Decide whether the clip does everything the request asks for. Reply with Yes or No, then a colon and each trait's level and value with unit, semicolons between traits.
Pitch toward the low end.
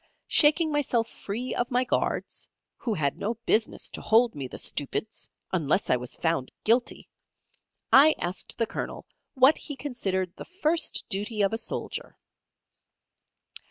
No: high, 225 Hz